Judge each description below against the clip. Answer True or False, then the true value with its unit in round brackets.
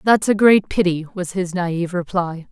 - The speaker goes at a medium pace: True (190 wpm)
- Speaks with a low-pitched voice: False (185 Hz)